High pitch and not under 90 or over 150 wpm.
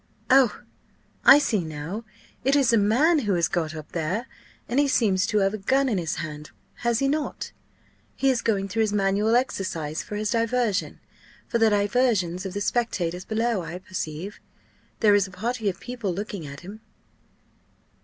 No: high, 205 Hz; average, 180 wpm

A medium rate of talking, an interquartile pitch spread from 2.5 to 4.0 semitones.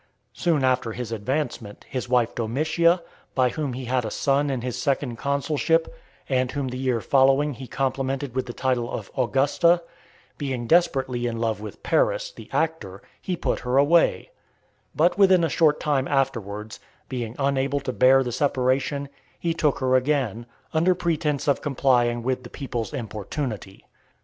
Yes: average, 160 wpm; average, 3.3 semitones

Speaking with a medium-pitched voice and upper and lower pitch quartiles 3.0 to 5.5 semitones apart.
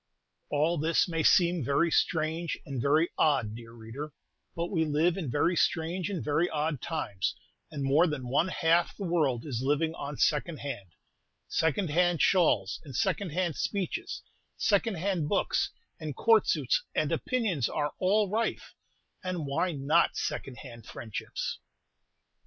Yes: medium, 160 Hz; average, 3.9 semitones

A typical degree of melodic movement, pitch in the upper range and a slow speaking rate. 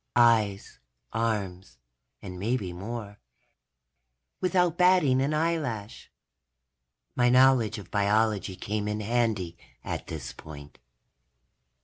No: average, 4.2 semitones; low, 110 Hz; slow, 95 wpm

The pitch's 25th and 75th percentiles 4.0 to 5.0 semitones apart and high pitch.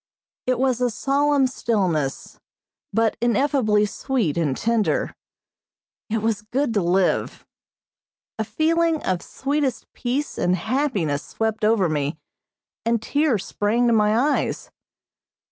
Yes: average, 4.6 semitones; high, 225 Hz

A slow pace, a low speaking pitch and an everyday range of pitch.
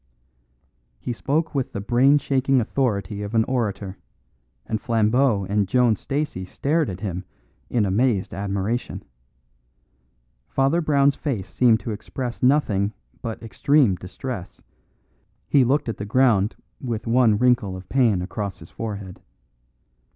Yes: slow, 130 wpm; low, 115 Hz; average, 4.8 semitones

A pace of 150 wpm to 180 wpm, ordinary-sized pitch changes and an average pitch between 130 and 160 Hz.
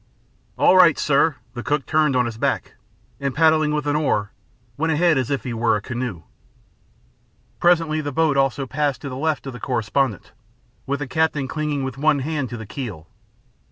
No: average, 190 wpm; average, 3.5 semitones; medium, 140 Hz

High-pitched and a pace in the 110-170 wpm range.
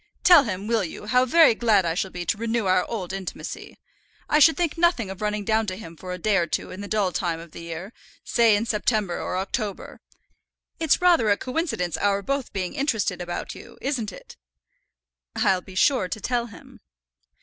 No: high, 210 Hz; fast, 205 wpm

